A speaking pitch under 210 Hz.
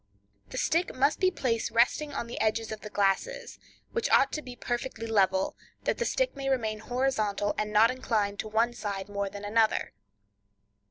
No: high, 230 Hz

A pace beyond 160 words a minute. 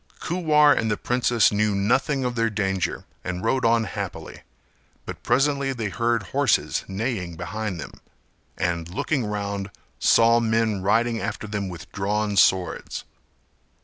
No: average, 140 wpm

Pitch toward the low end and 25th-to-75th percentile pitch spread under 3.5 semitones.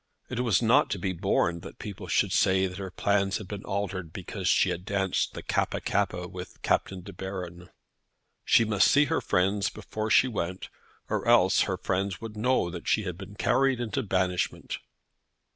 Yes: very low, 95 Hz; average, 2.8 semitones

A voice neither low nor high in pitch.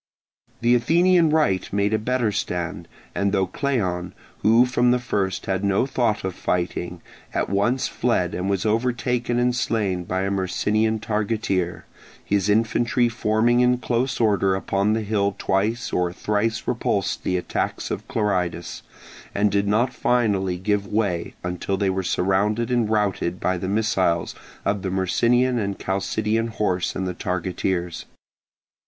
No: low, 105 Hz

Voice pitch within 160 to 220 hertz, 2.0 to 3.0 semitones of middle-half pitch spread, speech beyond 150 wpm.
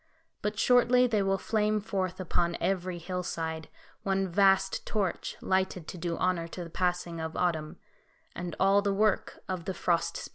Yes: medium, 185 Hz; narrow, 2.5 semitones; average, 170 wpm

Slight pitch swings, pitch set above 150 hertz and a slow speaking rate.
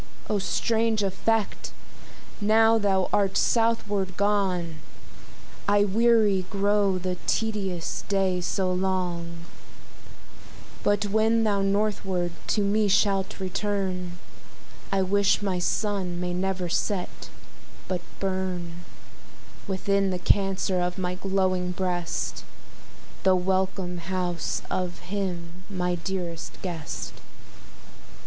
Yes: narrow, 2.1 semitones; high, 190 Hz; slow, 100 wpm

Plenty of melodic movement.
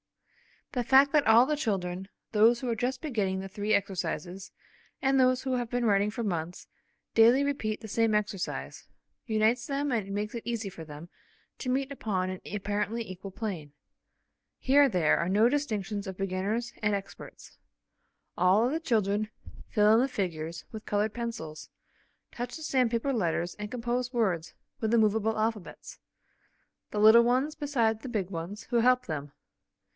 No: average, 3.9 semitones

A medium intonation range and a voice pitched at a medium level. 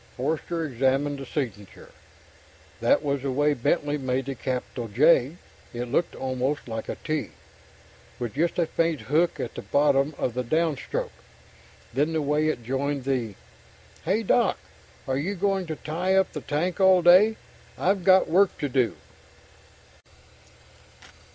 Yes: average, 4.5 semitones; medium, 145 Hz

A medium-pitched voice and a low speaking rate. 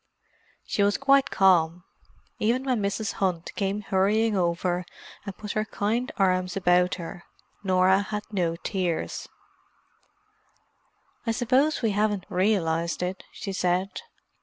No: high, 195 Hz; slow, 125 wpm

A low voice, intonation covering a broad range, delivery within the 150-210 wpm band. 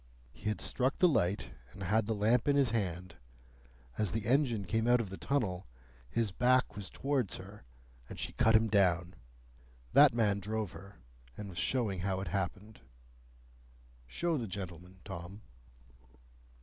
No: low, 105 Hz; average, 3.8 semitones; average, 160 wpm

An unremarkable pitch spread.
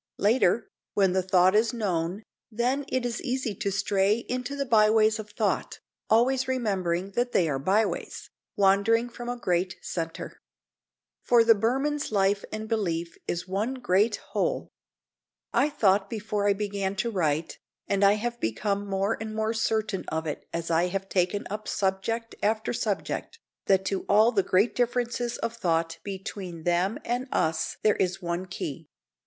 Yes: average, 3.6 semitones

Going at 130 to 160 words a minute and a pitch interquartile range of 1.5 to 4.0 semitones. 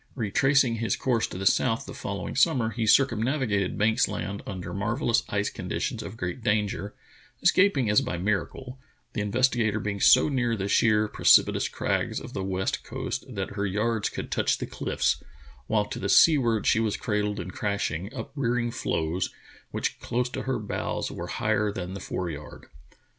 No: average, 170 wpm; average, 3.7 semitones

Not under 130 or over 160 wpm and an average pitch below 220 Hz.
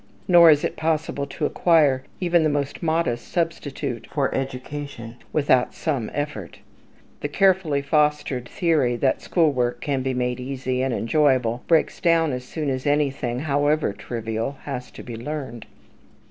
Yes: average, 150 wpm; medium, 140 Hz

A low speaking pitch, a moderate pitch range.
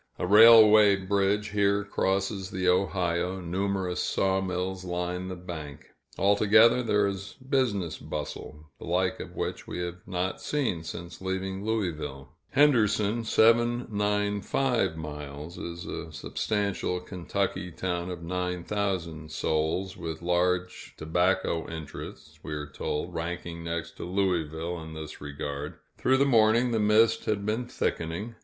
Yes: very low, 95 Hz; average, 3.4 semitones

